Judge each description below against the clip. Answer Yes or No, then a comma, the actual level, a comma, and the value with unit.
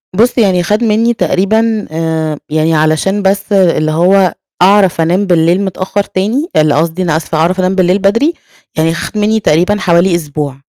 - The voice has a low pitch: No, medium, 185 Hz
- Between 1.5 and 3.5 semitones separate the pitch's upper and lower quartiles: No, average, 4.0 semitones